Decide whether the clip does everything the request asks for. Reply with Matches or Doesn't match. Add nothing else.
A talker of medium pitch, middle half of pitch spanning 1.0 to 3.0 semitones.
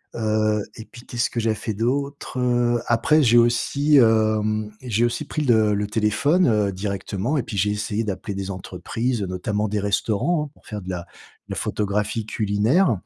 Doesn't match